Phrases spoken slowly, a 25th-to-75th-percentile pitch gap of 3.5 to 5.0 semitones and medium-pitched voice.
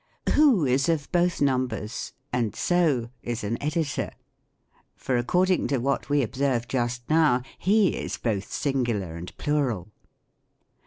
No: slow, 130 wpm; average, 4.5 semitones; low, 130 Hz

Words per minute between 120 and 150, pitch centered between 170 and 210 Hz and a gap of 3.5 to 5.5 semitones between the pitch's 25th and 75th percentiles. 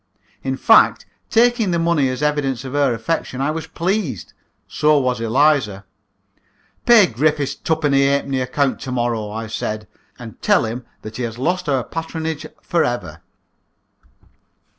No: average, 145 wpm; medium, 140 Hz; average, 4.8 semitones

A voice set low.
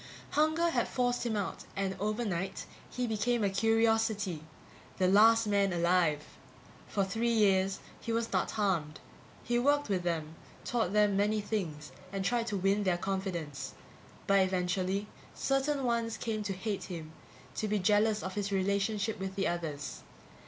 No: high, 200 Hz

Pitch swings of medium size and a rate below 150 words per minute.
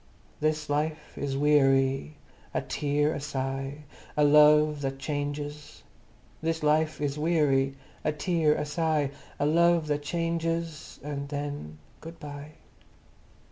No: narrow, 1.4 semitones; slow, 135 wpm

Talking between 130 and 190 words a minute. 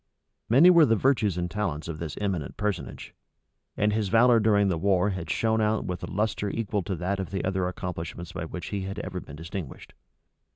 No: fast, 205 wpm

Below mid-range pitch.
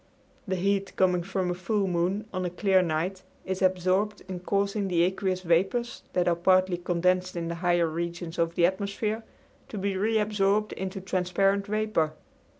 No: medium, 185 Hz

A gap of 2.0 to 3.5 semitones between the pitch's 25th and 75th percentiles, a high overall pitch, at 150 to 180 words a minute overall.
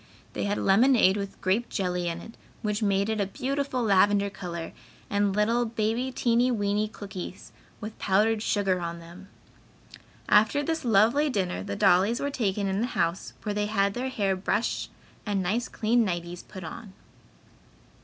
Yes: average, 3.2 semitones; high, 205 Hz; average, 165 wpm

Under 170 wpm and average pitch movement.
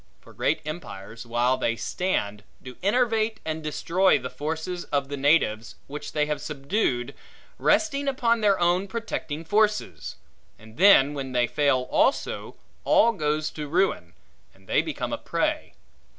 No: average, 150 wpm; wide, 7.1 semitones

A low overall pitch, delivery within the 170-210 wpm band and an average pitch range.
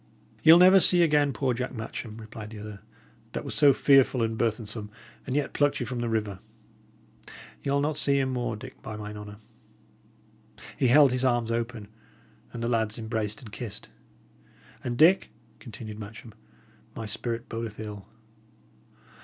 No: low, 115 Hz; average, 160 wpm; average, 3.6 semitones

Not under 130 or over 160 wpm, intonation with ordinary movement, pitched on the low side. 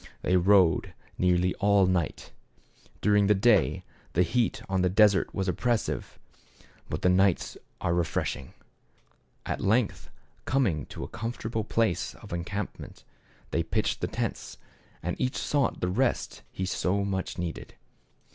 Yes: slow, 135 wpm; average, 3.4 semitones; very low, 95 Hz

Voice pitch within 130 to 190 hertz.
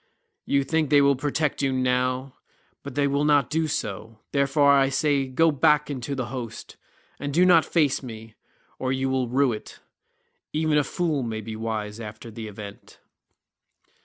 Yes: low, 135 Hz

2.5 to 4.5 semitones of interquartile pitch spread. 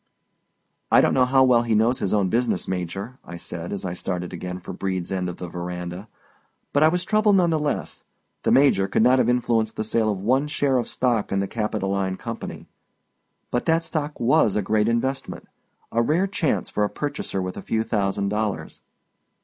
No: wide, 5.6 semitones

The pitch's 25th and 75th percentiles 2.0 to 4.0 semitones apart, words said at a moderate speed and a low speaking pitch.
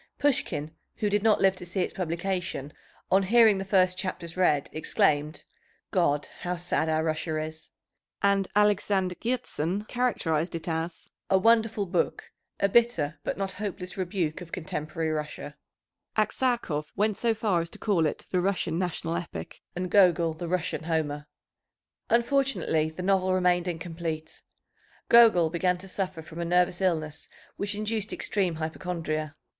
No: average, 3.6 semitones; average, 150 wpm; medium, 180 Hz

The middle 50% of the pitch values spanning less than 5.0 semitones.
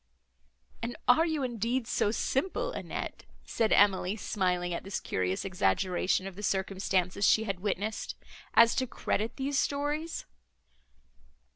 No: wide, 5.5 semitones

